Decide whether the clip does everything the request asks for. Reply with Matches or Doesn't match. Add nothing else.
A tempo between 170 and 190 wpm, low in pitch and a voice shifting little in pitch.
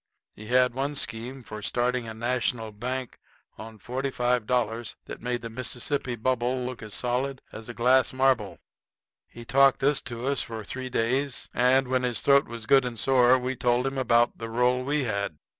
Matches